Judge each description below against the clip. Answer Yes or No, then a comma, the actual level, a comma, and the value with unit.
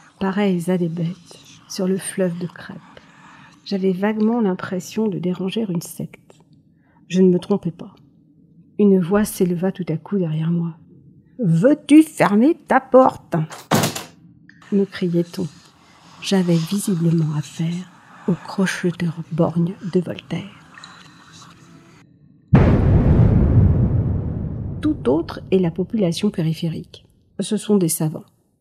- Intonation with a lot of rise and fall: No, average, 3.1 semitones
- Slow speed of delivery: Yes, slow, 110 wpm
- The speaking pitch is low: No, medium, 180 Hz